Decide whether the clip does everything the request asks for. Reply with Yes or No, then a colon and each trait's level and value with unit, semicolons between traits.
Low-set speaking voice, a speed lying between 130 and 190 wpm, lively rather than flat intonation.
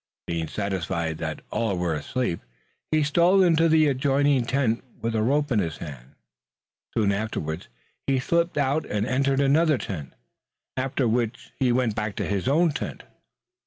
Yes: low, 125 Hz; average, 160 wpm; wide, 6.5 semitones